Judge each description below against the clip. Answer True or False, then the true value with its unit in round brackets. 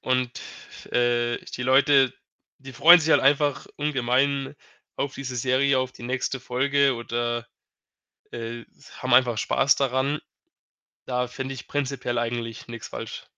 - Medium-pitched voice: False (130 Hz)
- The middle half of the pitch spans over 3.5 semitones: False (2.4 semitones)